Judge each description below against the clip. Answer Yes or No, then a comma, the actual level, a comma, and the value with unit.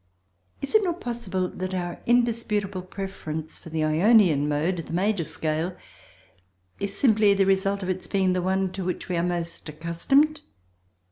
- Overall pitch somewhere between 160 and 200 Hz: Yes, medium, 185 Hz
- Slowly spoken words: No, average, 160 wpm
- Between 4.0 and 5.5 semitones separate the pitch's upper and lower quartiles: No, average, 3.4 semitones